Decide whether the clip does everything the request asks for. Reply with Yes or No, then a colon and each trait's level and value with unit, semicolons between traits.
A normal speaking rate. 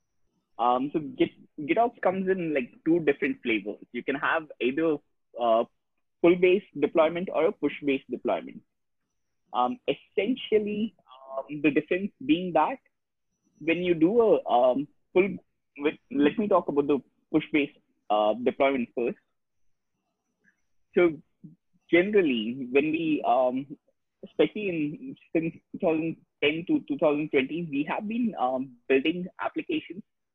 No: slow, 120 wpm